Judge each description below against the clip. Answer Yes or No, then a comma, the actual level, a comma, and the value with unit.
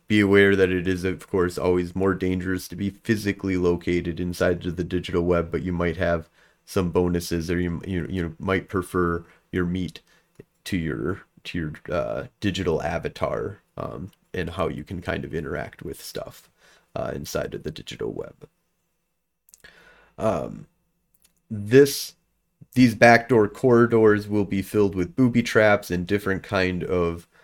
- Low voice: Yes, very low, 95 Hz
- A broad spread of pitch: No, average, 2.9 semitones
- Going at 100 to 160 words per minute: Yes, average, 155 wpm